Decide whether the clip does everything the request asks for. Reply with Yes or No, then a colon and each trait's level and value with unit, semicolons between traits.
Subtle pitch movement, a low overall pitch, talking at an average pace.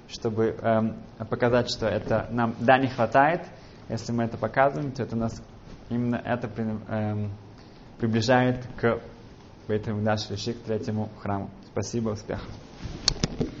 Yes: narrow, 1.8 semitones; low, 115 Hz; average, 120 wpm